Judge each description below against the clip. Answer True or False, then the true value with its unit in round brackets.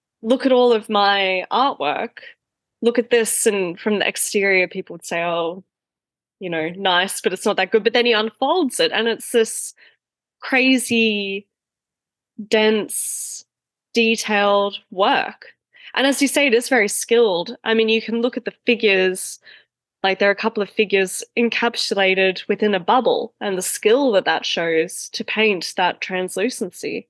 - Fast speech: False (165 wpm)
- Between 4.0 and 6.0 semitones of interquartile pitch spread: False (3.5 semitones)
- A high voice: True (215 Hz)